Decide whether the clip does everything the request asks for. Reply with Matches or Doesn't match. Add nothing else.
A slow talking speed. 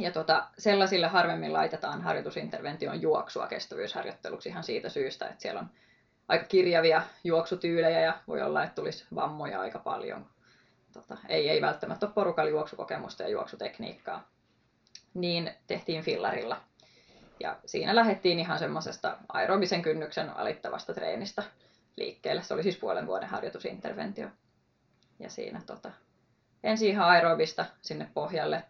Doesn't match